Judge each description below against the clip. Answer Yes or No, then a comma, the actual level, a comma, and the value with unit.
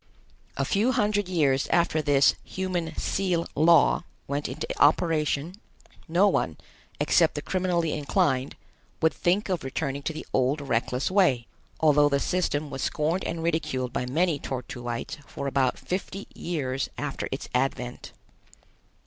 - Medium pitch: Yes, medium, 150 Hz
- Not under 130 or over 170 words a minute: Yes, average, 140 wpm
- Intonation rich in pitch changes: No, average, 4.4 semitones